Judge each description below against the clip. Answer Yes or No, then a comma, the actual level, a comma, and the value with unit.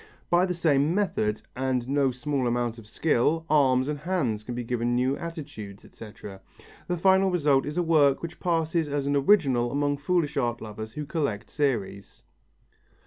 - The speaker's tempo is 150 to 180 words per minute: Yes, average, 170 wpm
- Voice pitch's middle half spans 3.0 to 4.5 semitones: No, average, 5.1 semitones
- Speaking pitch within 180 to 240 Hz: No, medium, 140 Hz